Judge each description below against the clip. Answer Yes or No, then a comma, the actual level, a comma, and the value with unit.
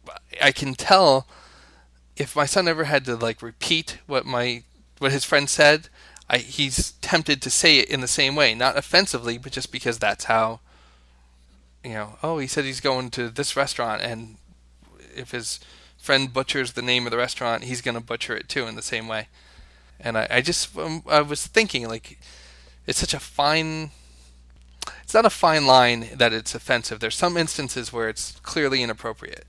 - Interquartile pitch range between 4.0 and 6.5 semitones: Yes, average, 4.6 semitones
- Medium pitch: No, low, 125 Hz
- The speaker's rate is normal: Yes, average, 185 wpm